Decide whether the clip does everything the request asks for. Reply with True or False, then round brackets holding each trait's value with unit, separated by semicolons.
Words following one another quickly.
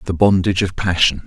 False (190 wpm)